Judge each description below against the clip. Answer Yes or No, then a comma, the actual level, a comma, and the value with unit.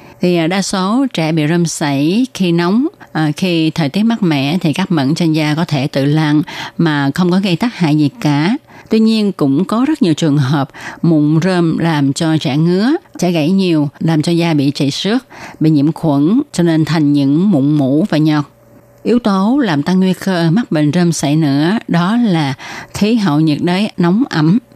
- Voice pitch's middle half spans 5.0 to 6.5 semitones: No, average, 4.2 semitones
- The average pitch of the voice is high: No, medium, 165 Hz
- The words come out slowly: No, average, 205 wpm